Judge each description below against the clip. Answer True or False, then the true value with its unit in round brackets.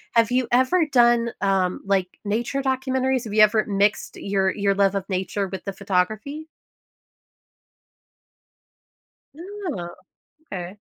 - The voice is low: False (210 Hz)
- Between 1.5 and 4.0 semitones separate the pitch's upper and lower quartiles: False (4.8 semitones)